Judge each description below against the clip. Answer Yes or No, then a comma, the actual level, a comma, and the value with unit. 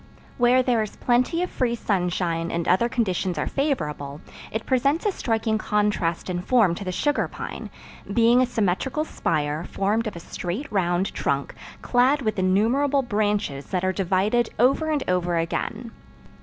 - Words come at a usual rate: Yes, average, 160 wpm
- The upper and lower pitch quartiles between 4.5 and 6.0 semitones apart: Yes, wide, 5.6 semitones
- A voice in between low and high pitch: No, high, 210 Hz